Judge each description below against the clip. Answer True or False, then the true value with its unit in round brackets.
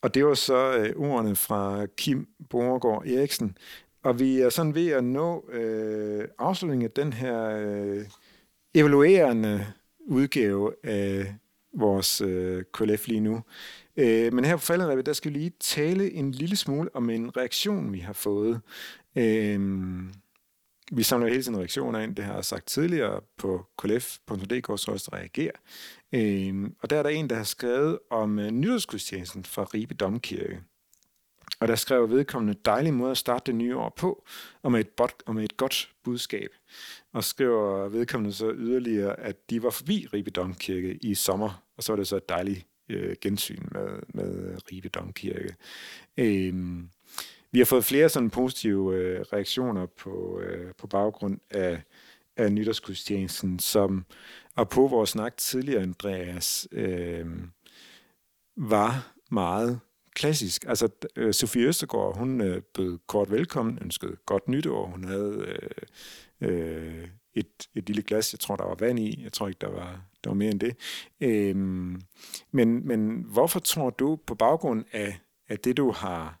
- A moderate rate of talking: True (160 wpm)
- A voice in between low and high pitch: False (110 Hz)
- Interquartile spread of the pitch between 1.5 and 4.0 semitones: False (4.4 semitones)